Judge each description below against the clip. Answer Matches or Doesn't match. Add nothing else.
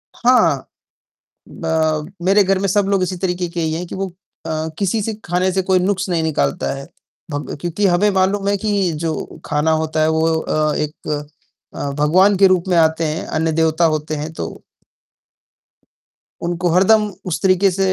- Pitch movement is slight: Doesn't match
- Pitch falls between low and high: Matches